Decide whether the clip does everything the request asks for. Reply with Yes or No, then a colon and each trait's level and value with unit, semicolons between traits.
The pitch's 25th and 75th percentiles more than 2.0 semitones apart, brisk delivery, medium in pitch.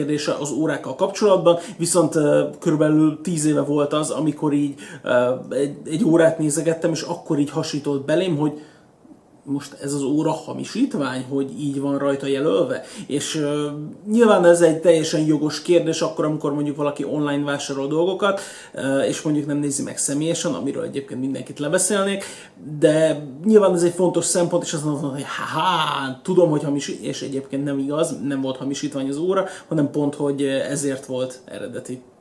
Yes: average, 2.9 semitones; fast, 160 wpm; medium, 150 Hz